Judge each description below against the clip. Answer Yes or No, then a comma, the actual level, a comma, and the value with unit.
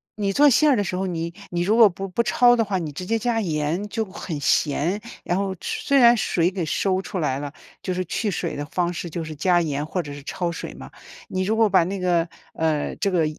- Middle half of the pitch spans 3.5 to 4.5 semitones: Yes, average, 3.9 semitones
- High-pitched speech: No, medium, 180 Hz